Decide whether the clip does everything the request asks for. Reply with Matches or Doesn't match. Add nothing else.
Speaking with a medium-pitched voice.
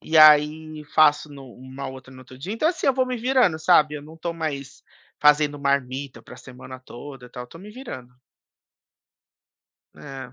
Matches